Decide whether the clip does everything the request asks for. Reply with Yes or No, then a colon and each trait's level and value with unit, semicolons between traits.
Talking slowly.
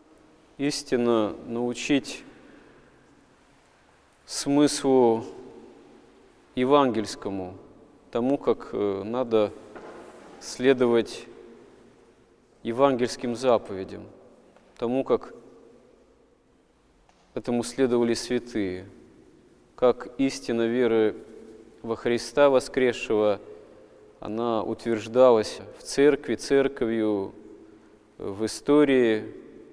Yes: slow, 55 wpm